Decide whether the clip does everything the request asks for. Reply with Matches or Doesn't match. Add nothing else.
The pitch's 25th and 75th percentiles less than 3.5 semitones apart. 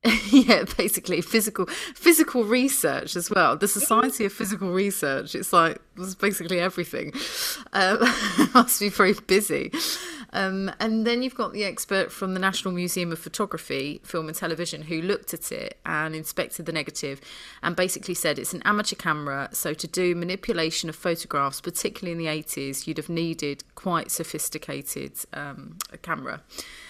Doesn't match